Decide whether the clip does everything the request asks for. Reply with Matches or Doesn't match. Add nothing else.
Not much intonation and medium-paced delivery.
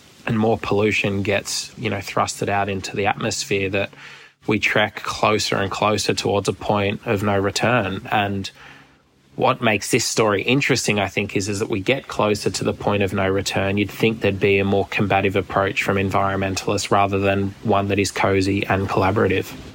Matches